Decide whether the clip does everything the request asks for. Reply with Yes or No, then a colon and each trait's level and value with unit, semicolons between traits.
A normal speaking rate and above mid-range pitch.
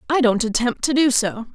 No: fast, 235 wpm; very high, 250 Hz